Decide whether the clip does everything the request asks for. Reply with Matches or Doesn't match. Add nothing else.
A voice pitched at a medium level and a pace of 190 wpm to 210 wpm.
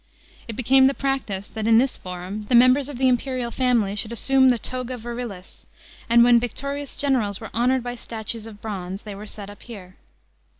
Doesn't match